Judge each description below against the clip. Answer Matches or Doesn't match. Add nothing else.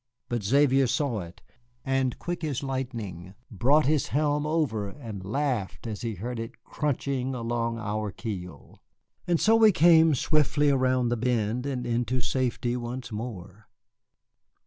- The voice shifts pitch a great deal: Doesn't match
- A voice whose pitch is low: Matches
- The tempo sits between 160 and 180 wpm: Doesn't match